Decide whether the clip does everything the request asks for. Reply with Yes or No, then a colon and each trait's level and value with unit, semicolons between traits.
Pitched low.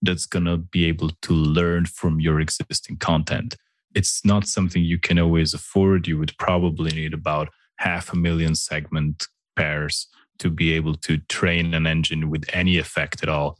Yes: very low, 80 Hz